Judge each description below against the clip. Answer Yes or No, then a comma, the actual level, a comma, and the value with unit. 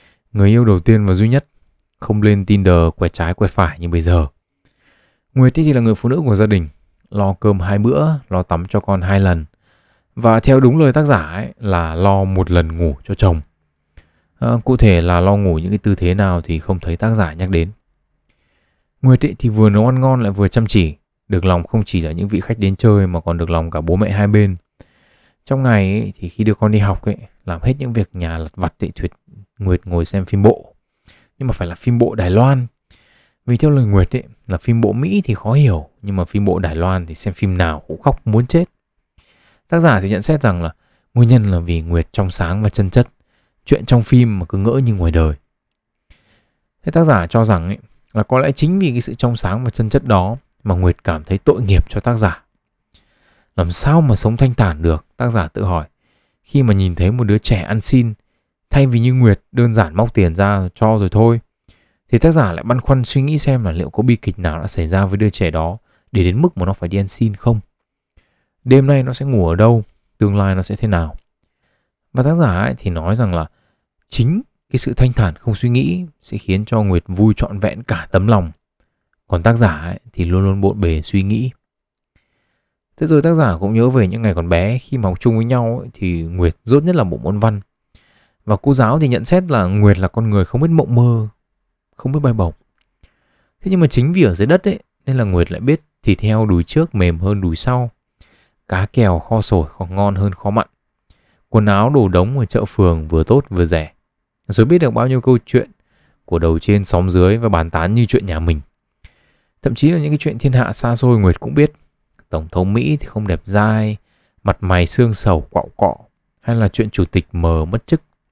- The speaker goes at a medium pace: Yes, average, 235 wpm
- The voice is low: Yes, low, 105 Hz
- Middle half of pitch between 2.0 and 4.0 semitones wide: No, average, 5.1 semitones